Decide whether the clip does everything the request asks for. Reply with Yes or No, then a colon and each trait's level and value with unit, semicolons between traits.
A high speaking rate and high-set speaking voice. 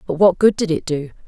No: fast, 285 wpm; medium, 175 Hz